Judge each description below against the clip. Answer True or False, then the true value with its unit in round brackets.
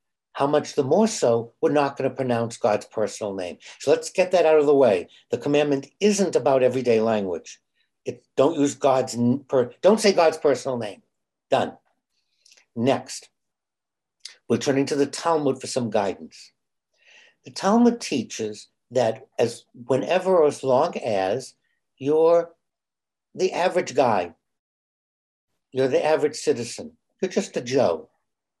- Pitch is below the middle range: False (145 Hz)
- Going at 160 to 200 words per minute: False (140 wpm)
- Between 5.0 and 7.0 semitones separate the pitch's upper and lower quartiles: True (5.6 semitones)